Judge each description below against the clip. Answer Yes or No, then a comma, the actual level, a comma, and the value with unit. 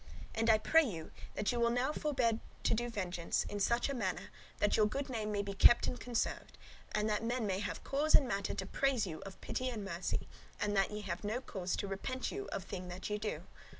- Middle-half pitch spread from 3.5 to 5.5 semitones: Yes, average, 3.9 semitones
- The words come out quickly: Yes, fast, 240 wpm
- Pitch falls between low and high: No, high, 215 Hz